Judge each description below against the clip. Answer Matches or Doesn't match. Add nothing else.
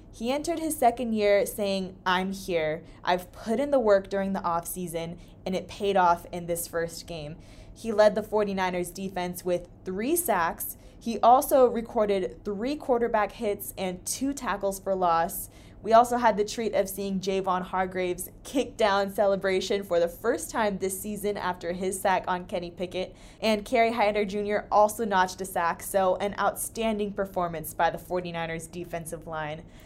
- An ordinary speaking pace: Matches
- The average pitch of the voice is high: Matches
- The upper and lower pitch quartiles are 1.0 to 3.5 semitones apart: Matches